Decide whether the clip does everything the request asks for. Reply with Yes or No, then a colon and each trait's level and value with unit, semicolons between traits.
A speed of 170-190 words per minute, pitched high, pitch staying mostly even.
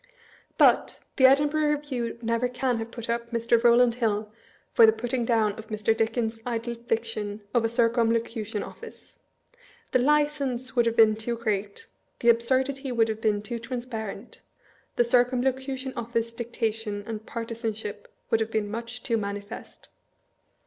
No: average, 155 wpm; high, 230 Hz; narrow, 1.8 semitones